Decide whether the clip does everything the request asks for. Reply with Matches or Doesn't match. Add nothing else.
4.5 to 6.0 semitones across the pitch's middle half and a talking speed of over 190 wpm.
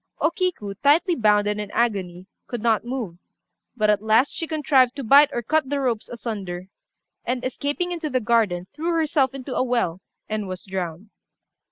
Doesn't match